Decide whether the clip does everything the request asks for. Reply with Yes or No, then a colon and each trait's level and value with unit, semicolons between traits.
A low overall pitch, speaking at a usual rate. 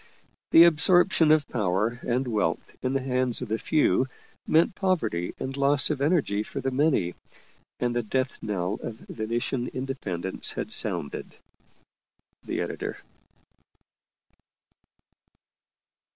No: low, 130 Hz; slow, 120 wpm